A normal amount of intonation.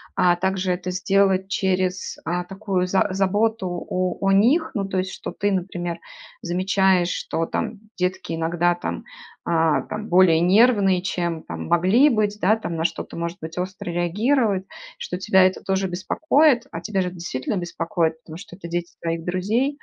No: narrow, 2.2 semitones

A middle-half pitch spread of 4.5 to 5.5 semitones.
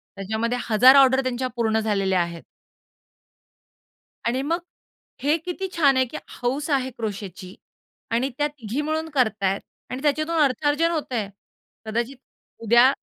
Yes: average, 4.9 semitones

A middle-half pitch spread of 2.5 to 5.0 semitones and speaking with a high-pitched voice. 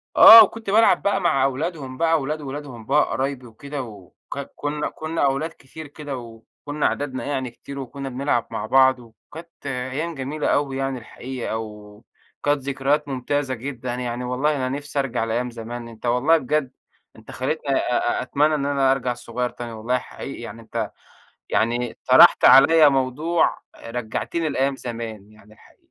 No: average, 3.2 semitones; low, 135 Hz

